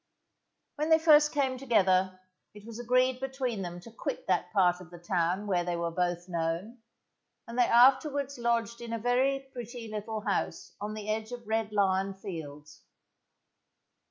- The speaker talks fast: No, average, 165 wpm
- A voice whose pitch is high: Yes, high, 215 Hz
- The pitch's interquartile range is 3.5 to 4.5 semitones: No, average, 5.1 semitones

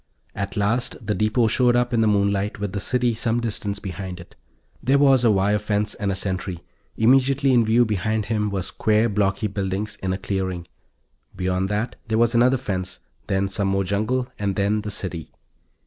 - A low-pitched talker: Yes, low, 105 Hz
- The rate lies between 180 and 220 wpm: Yes, average, 190 wpm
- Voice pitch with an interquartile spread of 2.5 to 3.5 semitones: Yes, average, 3.1 semitones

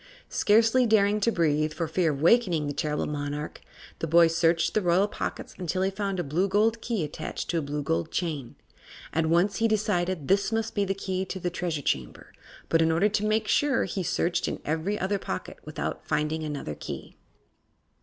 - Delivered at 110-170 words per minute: No, average, 200 wpm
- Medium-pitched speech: Yes, medium, 175 Hz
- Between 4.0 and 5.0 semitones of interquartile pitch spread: Yes, average, 4.6 semitones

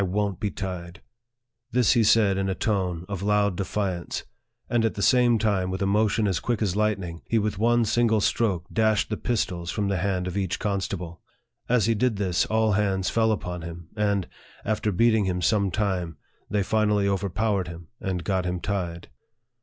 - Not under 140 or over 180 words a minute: No, average, 195 wpm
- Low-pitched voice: Yes, low, 100 Hz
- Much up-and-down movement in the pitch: No, average, 2.9 semitones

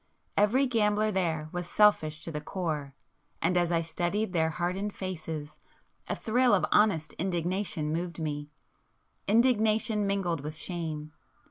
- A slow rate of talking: Yes, slow, 130 wpm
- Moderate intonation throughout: Yes, average, 4.7 semitones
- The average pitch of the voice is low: No, medium, 175 Hz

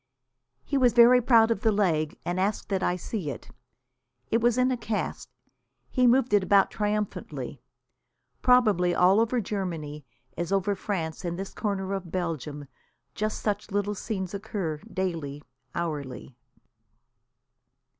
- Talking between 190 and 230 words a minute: No, average, 140 wpm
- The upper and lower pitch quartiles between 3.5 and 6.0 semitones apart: Yes, average, 4.3 semitones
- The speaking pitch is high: Yes, high, 195 Hz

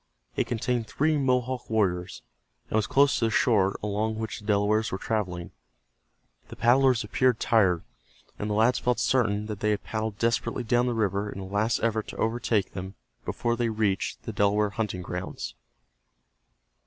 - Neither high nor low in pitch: No, low, 110 Hz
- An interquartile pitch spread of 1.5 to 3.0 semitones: Yes, narrow, 2.6 semitones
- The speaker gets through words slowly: No, average, 170 wpm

